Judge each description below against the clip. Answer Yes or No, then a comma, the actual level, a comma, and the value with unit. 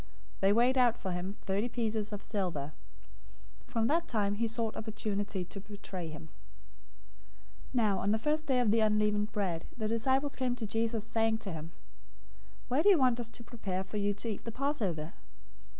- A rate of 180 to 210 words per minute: Yes, average, 185 wpm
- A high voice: Yes, high, 215 Hz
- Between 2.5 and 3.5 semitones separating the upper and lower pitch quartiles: Yes, average, 3.0 semitones